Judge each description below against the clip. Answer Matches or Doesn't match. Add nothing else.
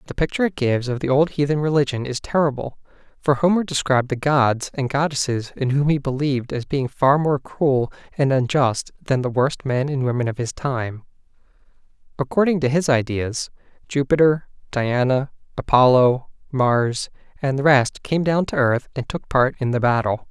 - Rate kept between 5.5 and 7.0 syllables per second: Doesn't match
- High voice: Doesn't match